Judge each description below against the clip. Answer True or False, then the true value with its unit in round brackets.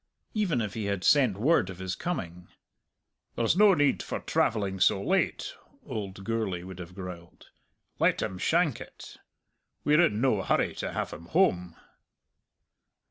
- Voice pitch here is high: False (105 Hz)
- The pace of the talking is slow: False (150 wpm)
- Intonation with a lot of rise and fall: True (7.9 semitones)